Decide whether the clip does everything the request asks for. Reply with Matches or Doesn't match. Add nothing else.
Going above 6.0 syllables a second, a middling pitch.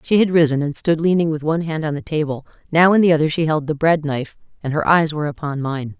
Matches